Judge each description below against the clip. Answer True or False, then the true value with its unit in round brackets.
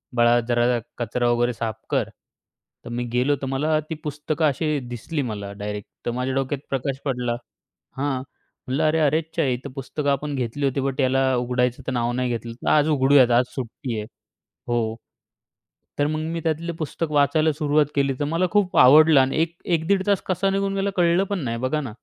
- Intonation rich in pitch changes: False (4.1 semitones)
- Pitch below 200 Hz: True (135 Hz)